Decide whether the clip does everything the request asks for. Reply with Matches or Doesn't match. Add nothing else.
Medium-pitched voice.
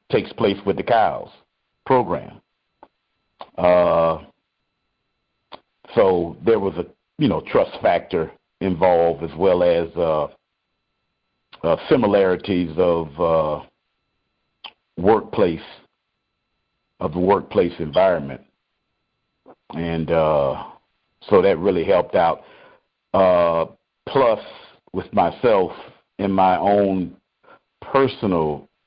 Doesn't match